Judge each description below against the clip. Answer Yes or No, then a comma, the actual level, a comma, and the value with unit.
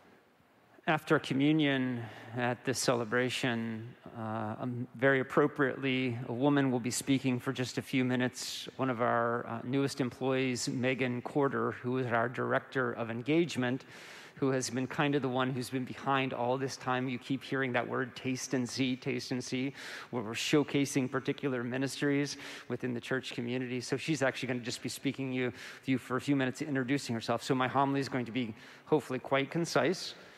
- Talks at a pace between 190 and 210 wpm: No, average, 180 wpm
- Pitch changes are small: Yes, narrow, 1.8 semitones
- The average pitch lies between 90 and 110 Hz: No, low, 130 Hz